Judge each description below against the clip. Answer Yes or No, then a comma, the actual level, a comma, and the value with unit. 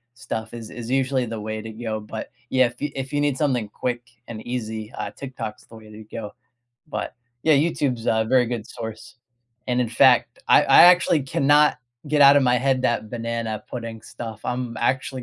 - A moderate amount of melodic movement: Yes, average, 3.0 semitones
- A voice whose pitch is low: Yes, low, 120 Hz